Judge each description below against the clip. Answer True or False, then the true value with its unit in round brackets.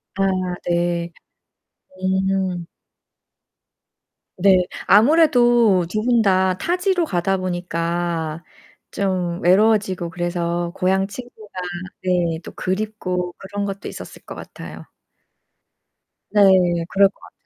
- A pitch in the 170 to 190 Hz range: True (185 Hz)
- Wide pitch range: False (3.1 semitones)